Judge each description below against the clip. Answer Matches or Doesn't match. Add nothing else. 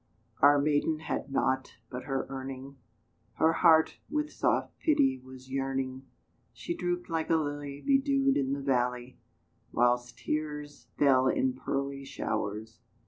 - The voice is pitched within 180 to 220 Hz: Doesn't match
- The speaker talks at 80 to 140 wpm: Matches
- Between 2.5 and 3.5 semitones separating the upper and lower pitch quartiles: Matches